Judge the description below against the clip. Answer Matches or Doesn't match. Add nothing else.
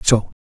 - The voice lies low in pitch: Matches